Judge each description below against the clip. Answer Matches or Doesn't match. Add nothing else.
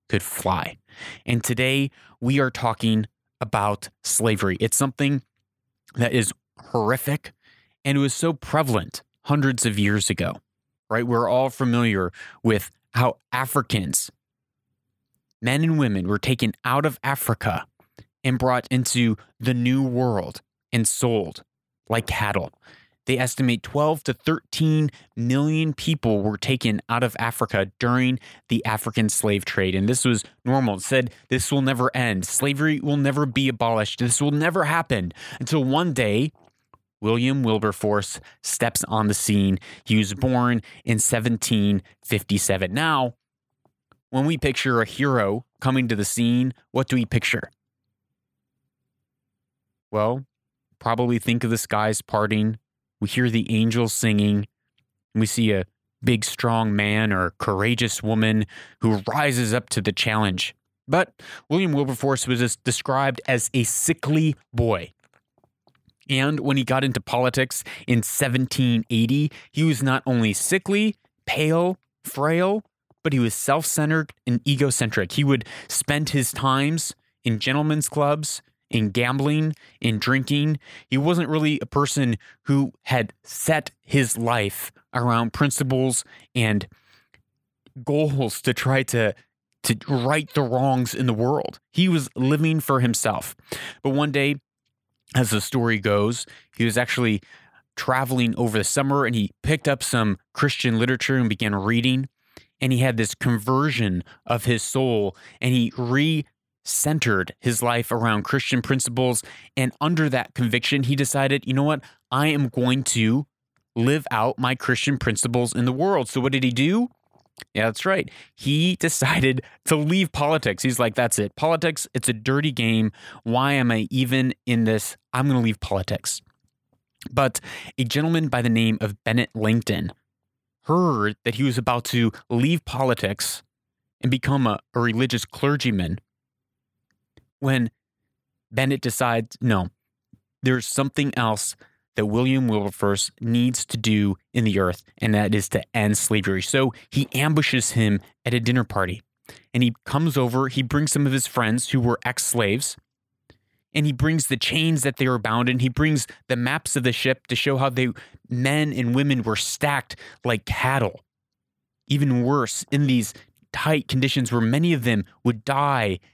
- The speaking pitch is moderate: Doesn't match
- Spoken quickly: Doesn't match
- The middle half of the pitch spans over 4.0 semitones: Doesn't match